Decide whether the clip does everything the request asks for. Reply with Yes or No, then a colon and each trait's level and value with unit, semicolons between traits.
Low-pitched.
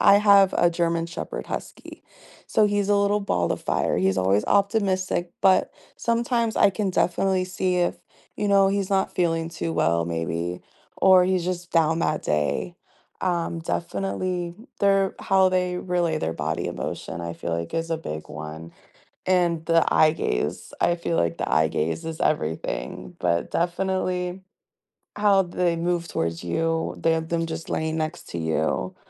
No: medium, 170 Hz